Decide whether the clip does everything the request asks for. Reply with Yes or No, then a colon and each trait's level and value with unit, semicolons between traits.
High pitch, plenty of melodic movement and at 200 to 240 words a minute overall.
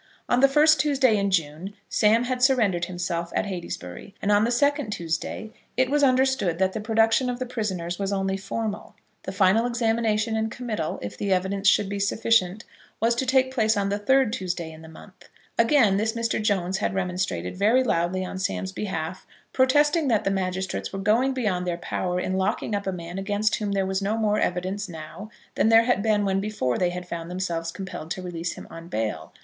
No: high, 200 Hz; average, 4.0 semitones; fast, 205 wpm